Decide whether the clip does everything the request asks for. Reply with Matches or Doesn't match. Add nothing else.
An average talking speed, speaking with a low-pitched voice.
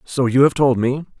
Doesn't match